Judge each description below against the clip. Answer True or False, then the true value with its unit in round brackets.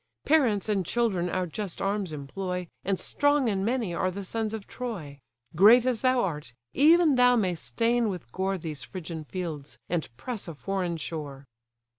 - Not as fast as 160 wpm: False (170 wpm)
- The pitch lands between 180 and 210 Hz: True (190 Hz)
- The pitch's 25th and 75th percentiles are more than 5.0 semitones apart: True (5.6 semitones)